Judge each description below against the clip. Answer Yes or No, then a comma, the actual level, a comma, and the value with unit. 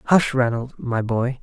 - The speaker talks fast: No, average, 170 wpm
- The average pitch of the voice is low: Yes, low, 125 Hz